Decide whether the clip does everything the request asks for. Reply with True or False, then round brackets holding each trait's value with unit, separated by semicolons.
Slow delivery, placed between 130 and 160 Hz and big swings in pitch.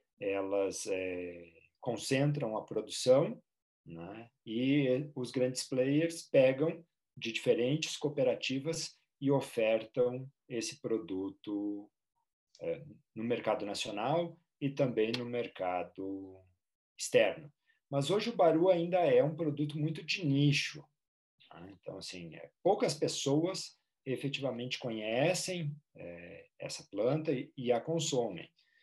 True (110 wpm; 135 Hz; 6.3 semitones)